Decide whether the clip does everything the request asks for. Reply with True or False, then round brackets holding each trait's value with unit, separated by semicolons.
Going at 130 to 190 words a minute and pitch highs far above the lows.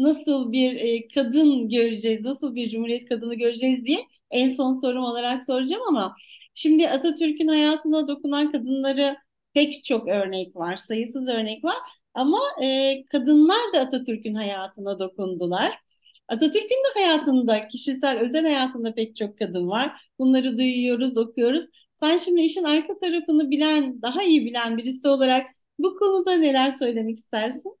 False (135 wpm; 4.6 semitones)